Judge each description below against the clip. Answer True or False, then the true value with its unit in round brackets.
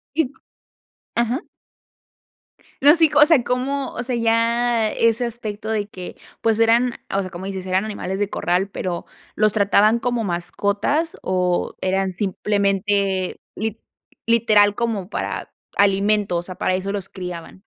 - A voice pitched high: True (205 Hz)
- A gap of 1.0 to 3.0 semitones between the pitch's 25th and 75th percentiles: False (3.5 semitones)